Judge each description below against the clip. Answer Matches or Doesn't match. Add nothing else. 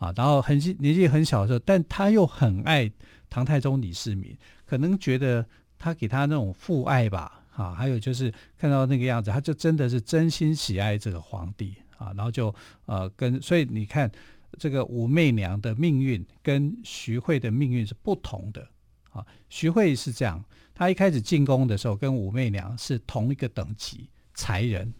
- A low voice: Matches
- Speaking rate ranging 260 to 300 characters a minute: Matches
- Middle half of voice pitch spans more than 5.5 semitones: Doesn't match